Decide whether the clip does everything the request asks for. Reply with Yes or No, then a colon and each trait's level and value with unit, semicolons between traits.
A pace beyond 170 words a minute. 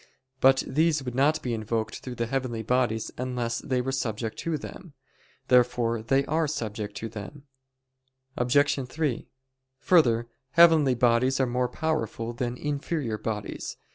No: average, 140 wpm